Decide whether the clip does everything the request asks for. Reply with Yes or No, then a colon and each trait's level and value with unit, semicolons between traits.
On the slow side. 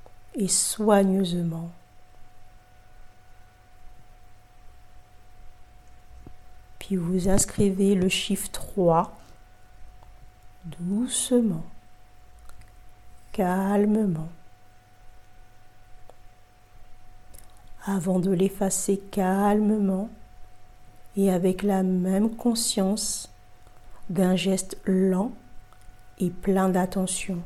Yes: slow, 55 wpm